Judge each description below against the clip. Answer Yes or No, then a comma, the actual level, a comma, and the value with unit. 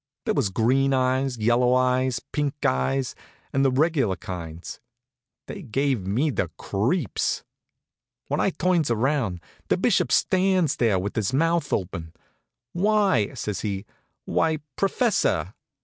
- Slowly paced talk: Yes, slow, 130 wpm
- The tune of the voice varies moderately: No, wide, 6.4 semitones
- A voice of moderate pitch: No, low, 130 Hz